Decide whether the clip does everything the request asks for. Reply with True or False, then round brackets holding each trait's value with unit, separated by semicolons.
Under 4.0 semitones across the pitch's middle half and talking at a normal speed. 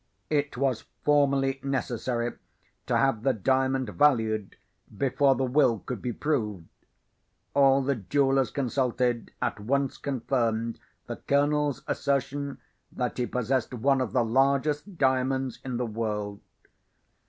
False (2.8 semitones; 125 wpm)